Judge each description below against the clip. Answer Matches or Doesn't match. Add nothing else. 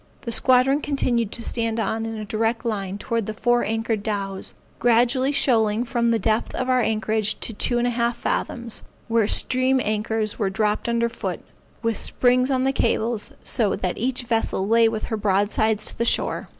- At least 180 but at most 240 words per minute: Matches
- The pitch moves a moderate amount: Doesn't match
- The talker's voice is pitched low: Doesn't match